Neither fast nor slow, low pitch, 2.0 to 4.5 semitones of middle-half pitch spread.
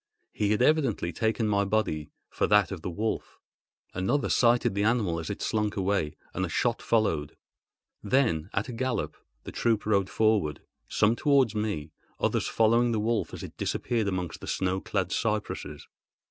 Yes: average, 165 wpm; low, 105 Hz; average, 3.5 semitones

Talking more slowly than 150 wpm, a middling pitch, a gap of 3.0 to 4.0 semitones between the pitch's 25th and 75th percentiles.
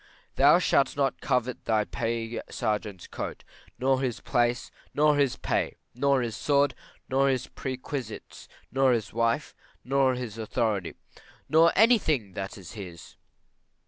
No: average, 140 wpm; low, 125 Hz; average, 3.6 semitones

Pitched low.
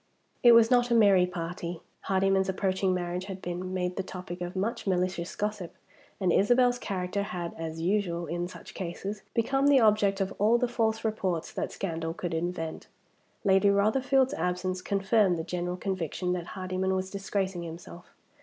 No: high, 190 Hz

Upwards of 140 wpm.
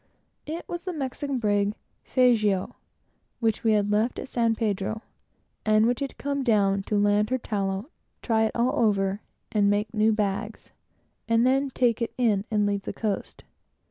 Yes: average, 170 wpm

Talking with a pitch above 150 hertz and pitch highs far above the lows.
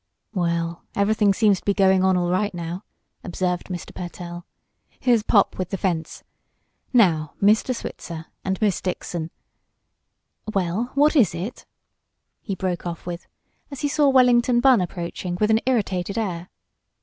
No: high, 190 Hz; average, 3.9 semitones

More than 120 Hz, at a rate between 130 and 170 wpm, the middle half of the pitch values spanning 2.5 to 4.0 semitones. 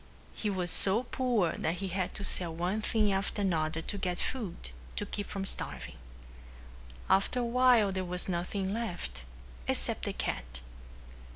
Yes: high, 190 Hz; average, 160 wpm; average, 3.3 semitones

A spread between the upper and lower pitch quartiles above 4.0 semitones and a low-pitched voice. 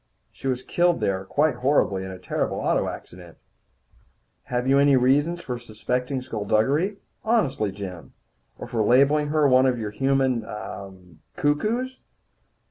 Yes: average, 5.3 semitones; low, 130 Hz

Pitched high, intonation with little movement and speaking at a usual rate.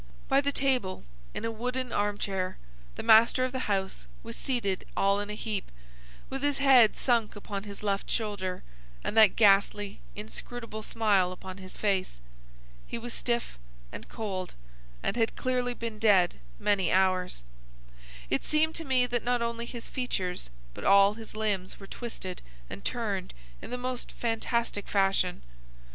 No: high, 215 Hz; average, 3.8 semitones; average, 160 wpm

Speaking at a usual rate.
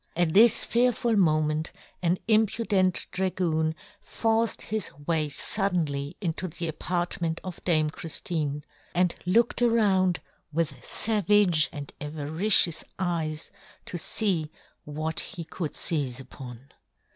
No: slow, 115 wpm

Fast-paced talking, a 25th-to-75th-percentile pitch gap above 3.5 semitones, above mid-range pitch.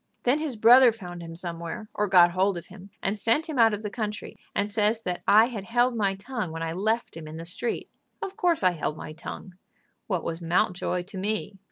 Yes: fast, 225 wpm; average, 4.4 semitones; high, 200 Hz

